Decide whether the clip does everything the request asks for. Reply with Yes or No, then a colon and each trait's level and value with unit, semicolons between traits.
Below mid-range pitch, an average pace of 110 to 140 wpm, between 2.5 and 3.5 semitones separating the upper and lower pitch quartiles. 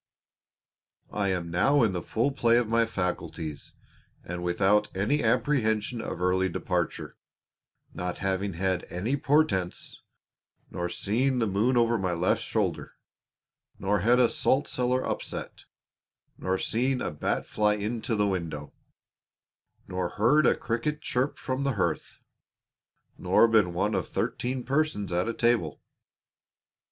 No: low, 105 Hz; slow, 135 wpm; average, 5.2 semitones